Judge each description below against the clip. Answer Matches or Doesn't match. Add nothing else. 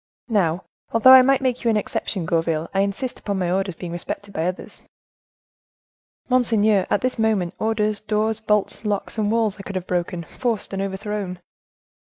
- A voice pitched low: Doesn't match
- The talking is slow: Doesn't match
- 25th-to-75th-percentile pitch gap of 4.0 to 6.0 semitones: Doesn't match